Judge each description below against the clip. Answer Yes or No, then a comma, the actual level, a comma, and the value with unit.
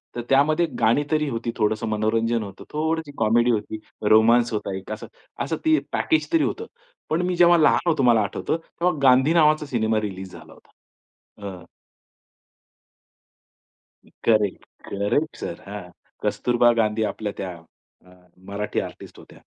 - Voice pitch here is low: Yes, low, 115 Hz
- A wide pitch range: Yes, wide, 6.2 semitones